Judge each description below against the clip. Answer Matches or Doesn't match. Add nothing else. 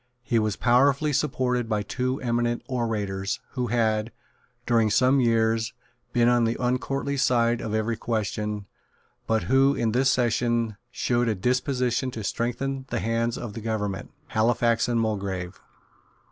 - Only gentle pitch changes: Matches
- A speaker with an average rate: Matches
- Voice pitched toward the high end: Doesn't match